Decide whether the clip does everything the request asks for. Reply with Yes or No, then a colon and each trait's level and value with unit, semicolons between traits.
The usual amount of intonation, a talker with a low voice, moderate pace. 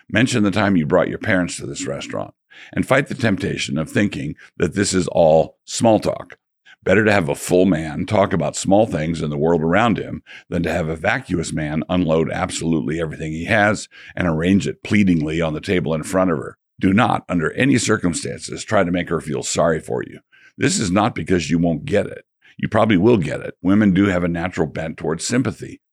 No: average, 3.5 semitones; very low, 90 Hz; fast, 215 wpm